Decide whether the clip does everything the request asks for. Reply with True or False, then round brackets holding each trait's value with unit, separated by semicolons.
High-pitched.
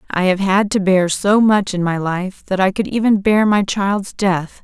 True (195 Hz)